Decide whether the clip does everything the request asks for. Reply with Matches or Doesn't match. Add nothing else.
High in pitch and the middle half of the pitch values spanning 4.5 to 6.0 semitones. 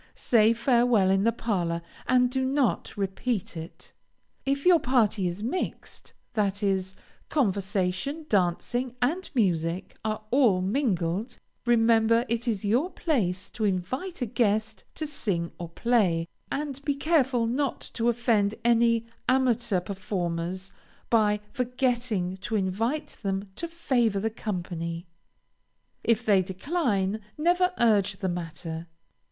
Matches